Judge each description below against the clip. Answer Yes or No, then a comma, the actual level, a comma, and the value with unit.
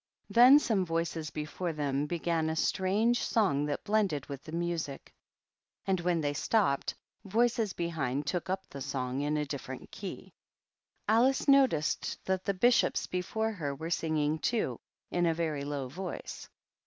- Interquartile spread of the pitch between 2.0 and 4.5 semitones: No, average, 5.1 semitones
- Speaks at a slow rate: No, average, 155 wpm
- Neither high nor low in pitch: Yes, medium, 165 Hz